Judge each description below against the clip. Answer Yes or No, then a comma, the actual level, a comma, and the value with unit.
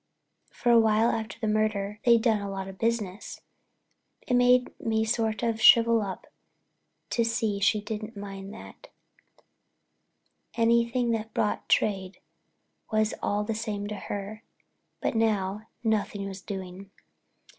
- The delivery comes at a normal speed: No, slow, 130 wpm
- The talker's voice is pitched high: Yes, high, 215 Hz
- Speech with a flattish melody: Yes, narrow, 2.1 semitones